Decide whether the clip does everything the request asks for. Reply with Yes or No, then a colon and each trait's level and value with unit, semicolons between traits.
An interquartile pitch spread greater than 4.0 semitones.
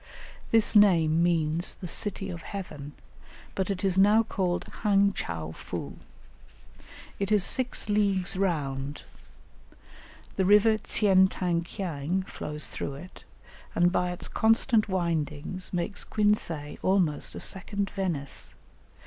No: average, 3.6 semitones